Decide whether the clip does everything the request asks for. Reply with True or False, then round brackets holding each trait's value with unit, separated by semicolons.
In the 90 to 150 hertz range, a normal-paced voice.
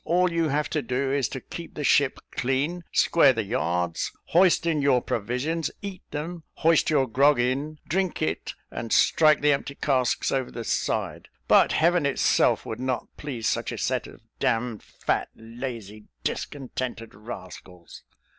True (135 Hz; 165 wpm)